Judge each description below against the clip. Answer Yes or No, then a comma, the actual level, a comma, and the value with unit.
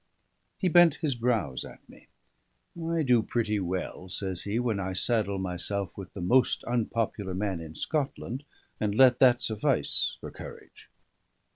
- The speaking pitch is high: No, low, 105 Hz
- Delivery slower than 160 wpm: Yes, average, 150 wpm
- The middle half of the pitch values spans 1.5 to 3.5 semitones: No, average, 4.7 semitones